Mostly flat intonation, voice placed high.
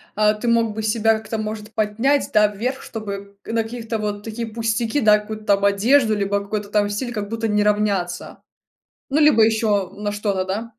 Yes: narrow, 1.7 semitones; high, 215 Hz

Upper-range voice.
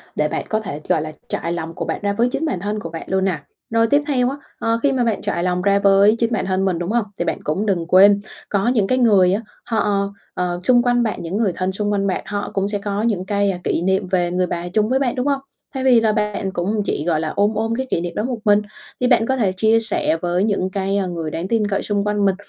Yes: high, 200 Hz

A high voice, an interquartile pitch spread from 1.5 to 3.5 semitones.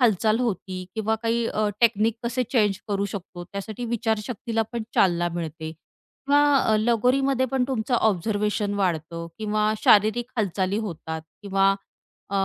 Yes: high, 215 Hz; average, 3.2 semitones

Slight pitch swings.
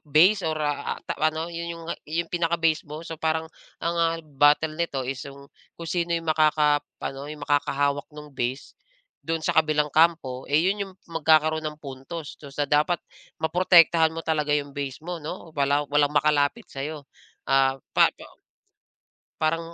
Yes: narrow, 2.3 semitones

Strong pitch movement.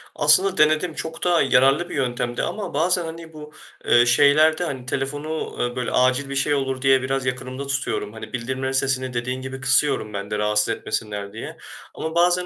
No: average, 3.5 semitones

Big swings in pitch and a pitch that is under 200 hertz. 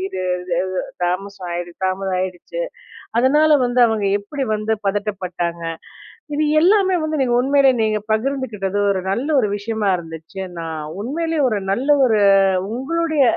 No: wide, 6.5 semitones; high, 215 Hz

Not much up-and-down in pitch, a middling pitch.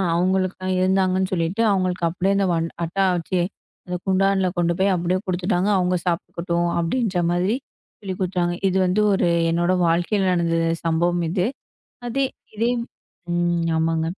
Yes: narrow, 1.7 semitones; medium, 180 Hz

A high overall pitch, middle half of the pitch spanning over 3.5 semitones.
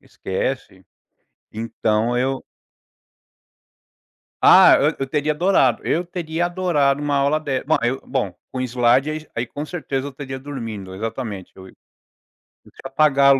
No: low, 135 Hz; average, 4.2 semitones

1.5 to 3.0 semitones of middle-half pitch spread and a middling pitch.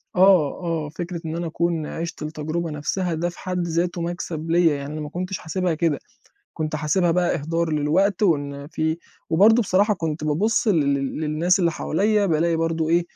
Yes: narrow, 2.5 semitones; medium, 165 Hz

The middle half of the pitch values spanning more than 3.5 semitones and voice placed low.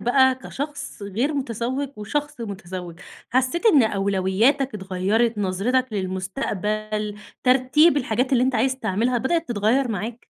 No: average, 4.5 semitones; high, 235 Hz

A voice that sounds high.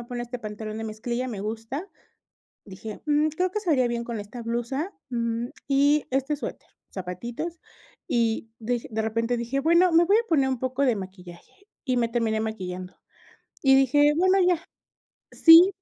Yes: high, 240 Hz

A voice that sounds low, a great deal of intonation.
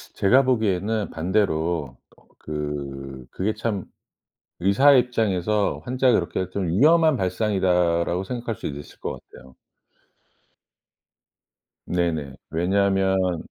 No: very low, 95 Hz; average, 4.6 semitones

